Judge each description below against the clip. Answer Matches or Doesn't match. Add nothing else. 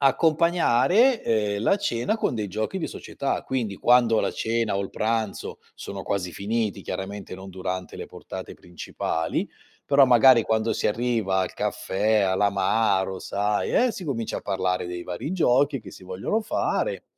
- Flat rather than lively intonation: Doesn't match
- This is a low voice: Matches